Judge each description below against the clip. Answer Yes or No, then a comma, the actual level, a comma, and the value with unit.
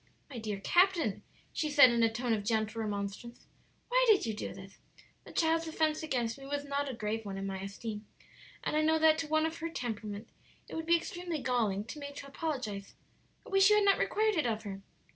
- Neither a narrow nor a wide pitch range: No, wide, 6.8 semitones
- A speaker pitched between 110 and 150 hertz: No, very high, 255 Hz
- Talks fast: Yes, fast, 225 wpm